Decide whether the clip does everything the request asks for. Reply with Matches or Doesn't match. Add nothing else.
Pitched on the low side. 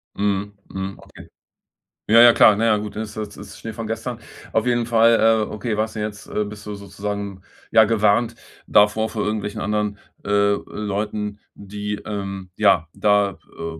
Matches